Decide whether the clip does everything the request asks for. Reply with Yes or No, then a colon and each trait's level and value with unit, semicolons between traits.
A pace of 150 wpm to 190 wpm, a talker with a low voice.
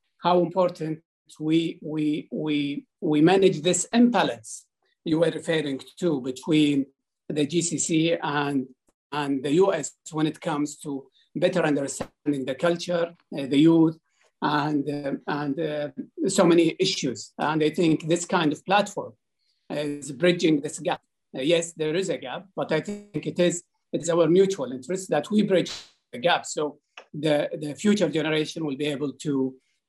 No: average, 155 wpm; medium, 155 Hz